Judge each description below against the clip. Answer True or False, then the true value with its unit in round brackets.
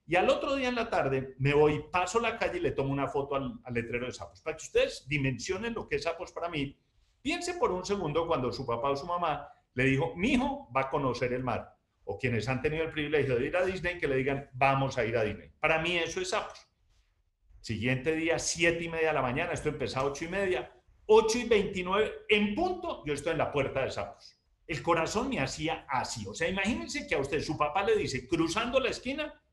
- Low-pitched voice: False (160 Hz)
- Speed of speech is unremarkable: False (240 wpm)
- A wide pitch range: True (6.6 semitones)